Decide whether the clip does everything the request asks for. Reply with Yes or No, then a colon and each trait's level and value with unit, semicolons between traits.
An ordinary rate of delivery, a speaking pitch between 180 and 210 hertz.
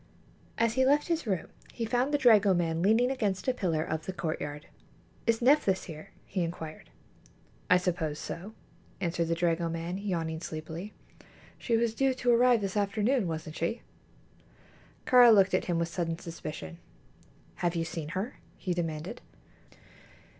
Yes: average, 150 wpm; medium, 185 Hz